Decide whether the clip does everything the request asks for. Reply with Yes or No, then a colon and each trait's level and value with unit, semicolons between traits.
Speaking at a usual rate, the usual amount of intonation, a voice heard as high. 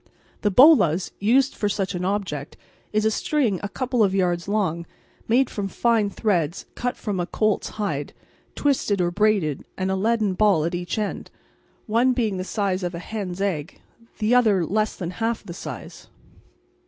Yes: average, 175 wpm; average, 3.4 semitones; high, 200 Hz